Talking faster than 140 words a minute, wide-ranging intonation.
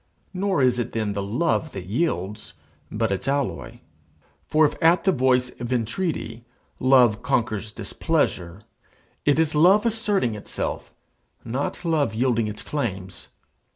No: slow, 135 wpm; wide, 6.3 semitones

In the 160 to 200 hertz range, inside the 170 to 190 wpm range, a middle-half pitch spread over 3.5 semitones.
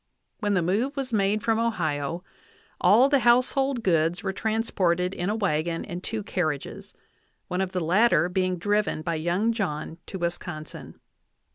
No: high, 190 Hz; average, 155 wpm; average, 4.5 semitones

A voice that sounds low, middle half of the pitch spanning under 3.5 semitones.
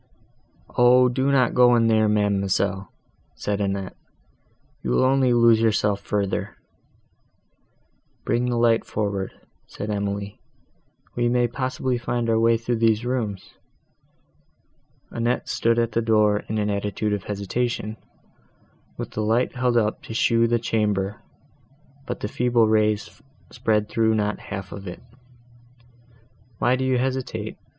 Yes: low, 110 Hz; average, 2.7 semitones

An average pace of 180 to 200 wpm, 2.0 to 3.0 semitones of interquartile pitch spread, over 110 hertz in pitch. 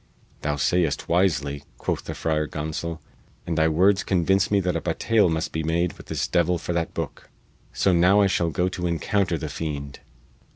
No: average, 190 wpm; narrow, 2.6 semitones; very low, 85 Hz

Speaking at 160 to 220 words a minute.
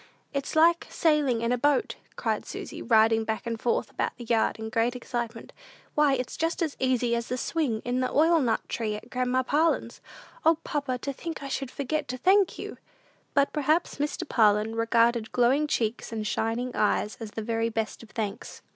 Yes: average, 190 wpm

